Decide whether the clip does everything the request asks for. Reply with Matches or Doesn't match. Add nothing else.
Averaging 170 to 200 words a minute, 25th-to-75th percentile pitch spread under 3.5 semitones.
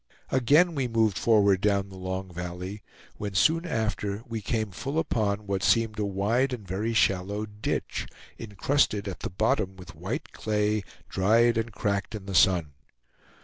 Doesn't match